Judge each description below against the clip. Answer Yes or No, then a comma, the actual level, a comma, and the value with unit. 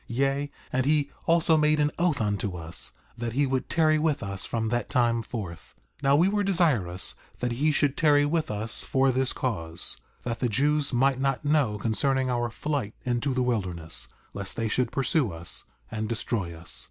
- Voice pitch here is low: Yes, low, 125 Hz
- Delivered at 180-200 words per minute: Yes, average, 190 wpm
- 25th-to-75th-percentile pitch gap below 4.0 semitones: No, average, 4.9 semitones